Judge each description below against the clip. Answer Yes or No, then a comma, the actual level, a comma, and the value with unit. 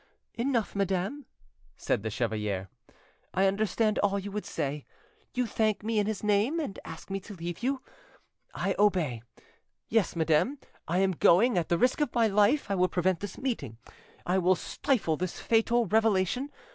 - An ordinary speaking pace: Yes, average, 170 wpm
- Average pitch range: Yes, average, 4.4 semitones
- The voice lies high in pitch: Yes, high, 200 Hz